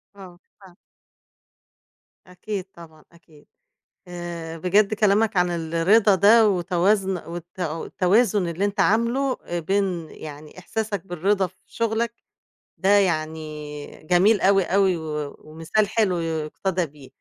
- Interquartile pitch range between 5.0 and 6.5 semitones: No, average, 3.7 semitones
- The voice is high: No, medium, 180 Hz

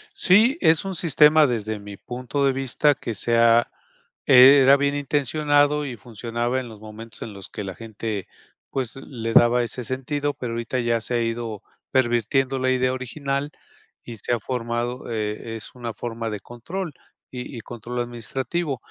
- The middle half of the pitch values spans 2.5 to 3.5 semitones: Yes, average, 3.1 semitones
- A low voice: Yes, low, 125 Hz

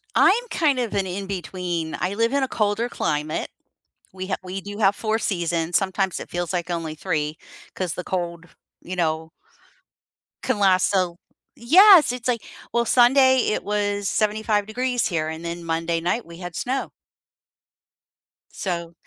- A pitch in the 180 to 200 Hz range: Yes, high, 190 Hz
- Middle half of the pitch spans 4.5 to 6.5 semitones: Yes, average, 5.1 semitones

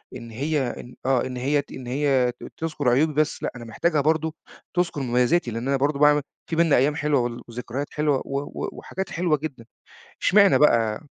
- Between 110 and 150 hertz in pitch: Yes, medium, 140 Hz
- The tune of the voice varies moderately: Yes, average, 3.7 semitones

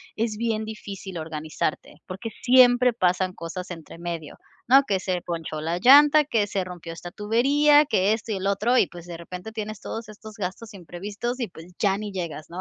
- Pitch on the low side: No, high, 200 Hz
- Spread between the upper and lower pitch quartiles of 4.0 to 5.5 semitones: Yes, average, 4.5 semitones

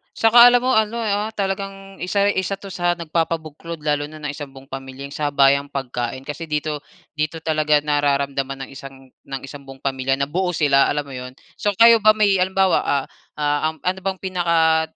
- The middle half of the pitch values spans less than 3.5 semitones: No, wide, 5.4 semitones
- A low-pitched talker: No, medium, 155 Hz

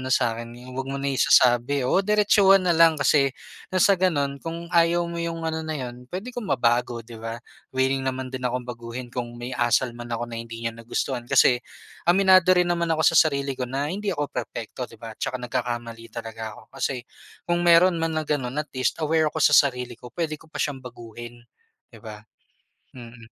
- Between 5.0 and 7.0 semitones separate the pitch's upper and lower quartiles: Yes, average, 5.3 semitones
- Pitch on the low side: Yes, low, 130 Hz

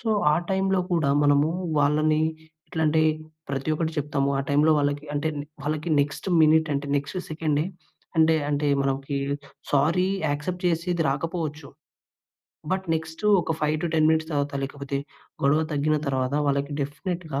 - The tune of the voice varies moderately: No, narrow, 2.1 semitones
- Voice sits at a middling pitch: Yes, medium, 150 Hz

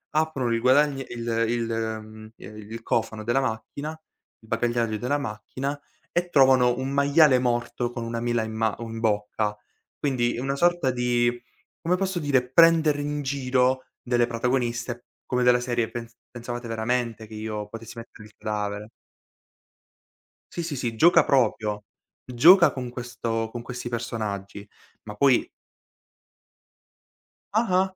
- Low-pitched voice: Yes, low, 120 Hz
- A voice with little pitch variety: No, average, 3.1 semitones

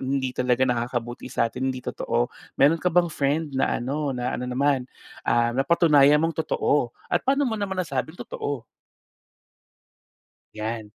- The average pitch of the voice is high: No, low, 135 Hz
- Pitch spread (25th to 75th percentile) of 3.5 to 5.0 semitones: Yes, average, 4.2 semitones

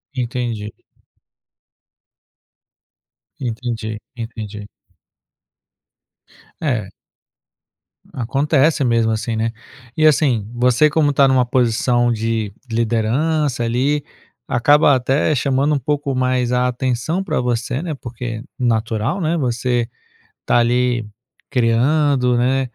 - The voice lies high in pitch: No, low, 125 Hz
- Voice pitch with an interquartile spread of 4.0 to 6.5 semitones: No, average, 3.2 semitones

